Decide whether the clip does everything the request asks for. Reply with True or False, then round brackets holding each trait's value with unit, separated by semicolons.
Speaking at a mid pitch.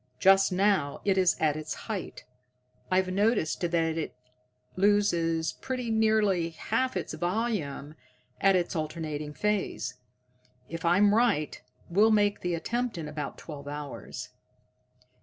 True (180 Hz)